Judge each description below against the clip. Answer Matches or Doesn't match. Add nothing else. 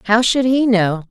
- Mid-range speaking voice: Doesn't match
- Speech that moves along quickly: Matches